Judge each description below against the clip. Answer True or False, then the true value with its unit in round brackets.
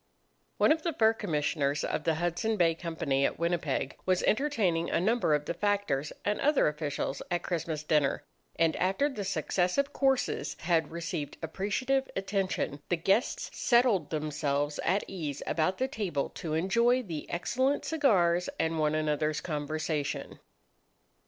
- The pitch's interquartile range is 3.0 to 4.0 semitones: False (5.3 semitones)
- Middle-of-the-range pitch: True (170 Hz)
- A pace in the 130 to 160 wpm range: True (150 wpm)